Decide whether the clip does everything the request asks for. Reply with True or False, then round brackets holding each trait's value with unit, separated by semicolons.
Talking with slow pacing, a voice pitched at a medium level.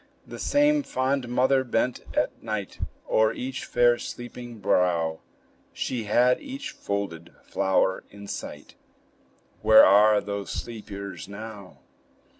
False (115 wpm; 110 Hz)